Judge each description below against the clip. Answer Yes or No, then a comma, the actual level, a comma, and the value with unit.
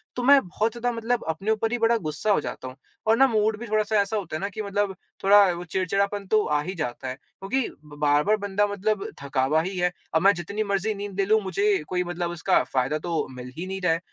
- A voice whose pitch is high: Yes, high, 195 Hz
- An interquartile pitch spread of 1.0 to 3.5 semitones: No, average, 4.0 semitones